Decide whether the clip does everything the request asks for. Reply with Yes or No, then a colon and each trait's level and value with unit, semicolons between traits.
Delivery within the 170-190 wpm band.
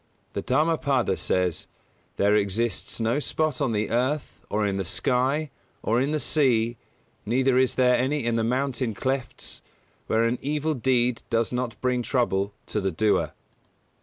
No: average, 160 wpm